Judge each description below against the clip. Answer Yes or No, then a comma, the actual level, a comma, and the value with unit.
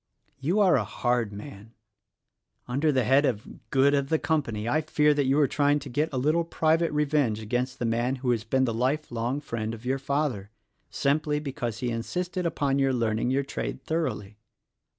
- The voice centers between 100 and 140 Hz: Yes, low, 135 Hz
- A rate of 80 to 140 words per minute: No, average, 195 wpm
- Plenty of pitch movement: No, average, 4.1 semitones